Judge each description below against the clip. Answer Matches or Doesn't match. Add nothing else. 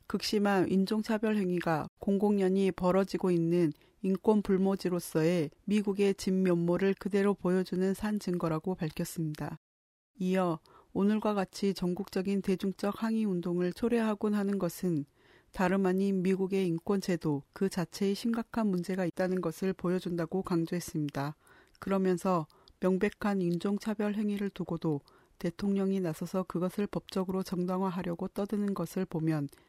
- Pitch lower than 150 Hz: Doesn't match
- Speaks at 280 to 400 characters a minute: Matches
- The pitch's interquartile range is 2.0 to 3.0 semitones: Matches